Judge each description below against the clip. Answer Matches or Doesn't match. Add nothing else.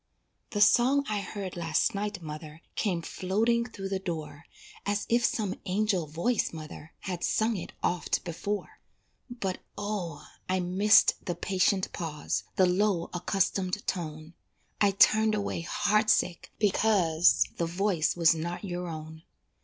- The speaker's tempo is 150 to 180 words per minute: Doesn't match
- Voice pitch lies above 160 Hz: Matches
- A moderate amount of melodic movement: Matches